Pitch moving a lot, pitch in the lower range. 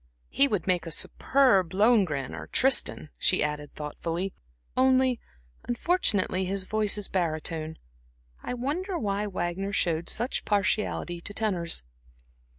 No: wide, 5.9 semitones; high, 195 Hz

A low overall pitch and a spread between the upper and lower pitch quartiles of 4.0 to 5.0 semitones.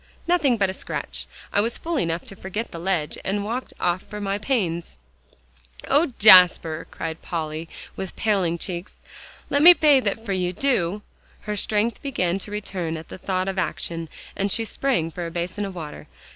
No: high, 190 Hz; average, 4.4 semitones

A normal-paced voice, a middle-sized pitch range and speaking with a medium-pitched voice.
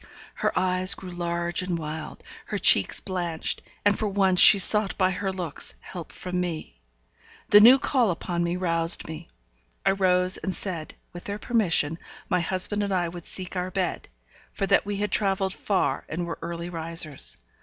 No: average, 175 wpm; narrow, 2.3 semitones; medium, 180 Hz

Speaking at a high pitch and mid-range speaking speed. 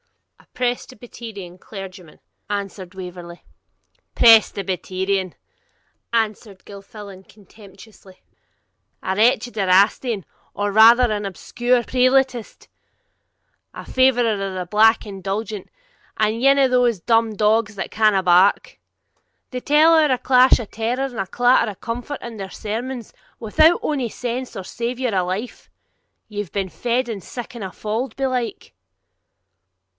No: high, 220 Hz; slow, 120 wpm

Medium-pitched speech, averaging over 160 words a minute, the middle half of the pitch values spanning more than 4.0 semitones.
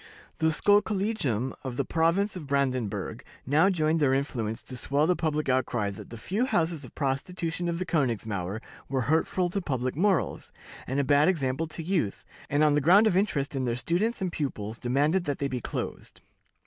Yes: medium, 145 Hz; average, 185 wpm; average, 5.2 semitones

